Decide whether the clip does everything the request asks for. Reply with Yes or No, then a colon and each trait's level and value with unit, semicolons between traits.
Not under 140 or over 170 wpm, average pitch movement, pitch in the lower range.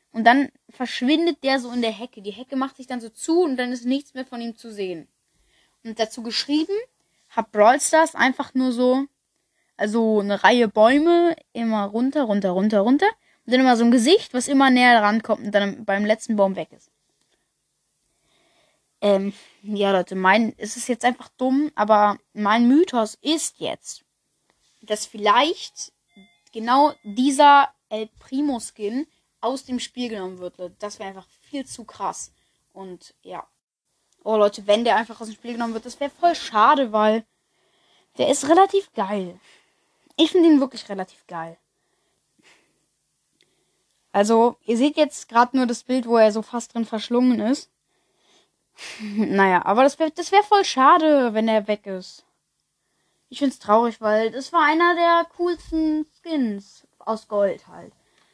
No: average, 165 wpm; average, 4.7 semitones; high, 235 Hz